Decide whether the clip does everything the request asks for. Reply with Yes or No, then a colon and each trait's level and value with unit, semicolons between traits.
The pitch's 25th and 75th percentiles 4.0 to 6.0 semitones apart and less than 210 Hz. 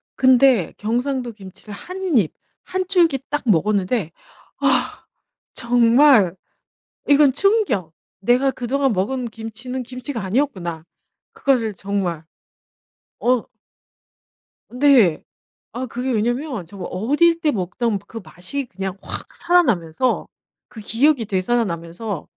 No: wide, 5.4 semitones; high, 235 Hz